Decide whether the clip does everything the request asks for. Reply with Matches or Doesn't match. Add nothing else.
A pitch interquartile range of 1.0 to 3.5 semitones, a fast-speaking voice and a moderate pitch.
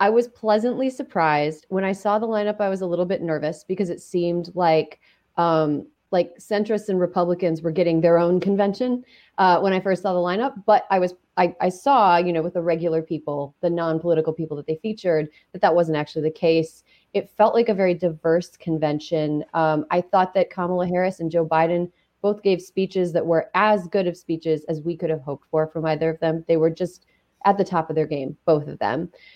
Matches